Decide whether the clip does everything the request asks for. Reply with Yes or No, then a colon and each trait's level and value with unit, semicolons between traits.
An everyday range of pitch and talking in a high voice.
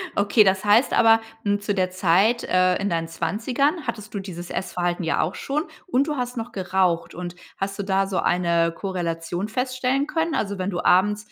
Yes: average, 4.4 semitones; high, 195 Hz